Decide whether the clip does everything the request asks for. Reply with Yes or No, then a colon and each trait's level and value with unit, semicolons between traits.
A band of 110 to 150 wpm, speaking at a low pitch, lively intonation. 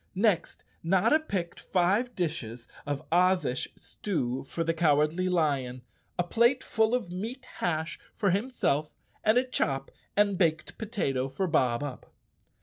No: average, 140 wpm; medium, 175 Hz; wide, 6.1 semitones